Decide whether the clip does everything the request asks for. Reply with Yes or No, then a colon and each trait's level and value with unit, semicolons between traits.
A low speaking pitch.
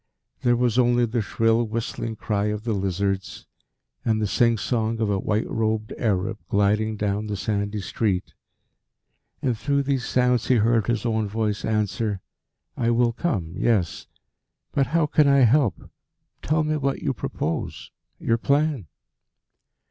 Yes: low, 110 Hz